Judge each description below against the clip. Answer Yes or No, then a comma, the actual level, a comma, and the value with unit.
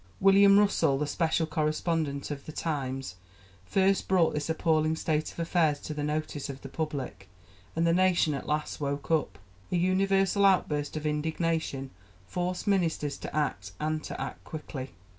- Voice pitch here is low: No, medium, 155 Hz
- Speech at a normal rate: Yes, average, 160 wpm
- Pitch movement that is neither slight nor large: Yes, average, 3.0 semitones